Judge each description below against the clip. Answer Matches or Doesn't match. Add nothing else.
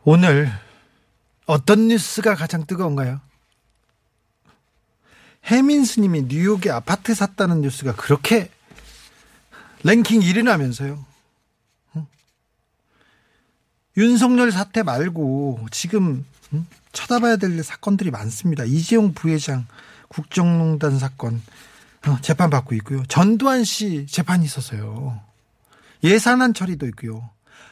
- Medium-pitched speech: Matches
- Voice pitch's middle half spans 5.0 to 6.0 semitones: Doesn't match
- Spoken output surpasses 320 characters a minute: Doesn't match